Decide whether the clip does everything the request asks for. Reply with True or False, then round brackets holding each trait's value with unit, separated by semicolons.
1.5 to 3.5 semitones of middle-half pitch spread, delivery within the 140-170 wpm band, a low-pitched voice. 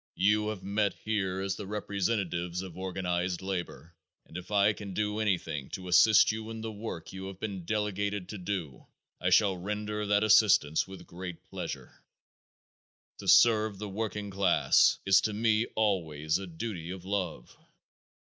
True (2.7 semitones; 160 wpm; 100 Hz)